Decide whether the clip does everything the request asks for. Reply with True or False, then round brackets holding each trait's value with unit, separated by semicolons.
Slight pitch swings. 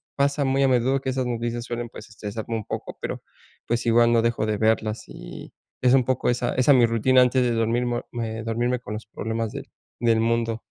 True (1.7 semitones)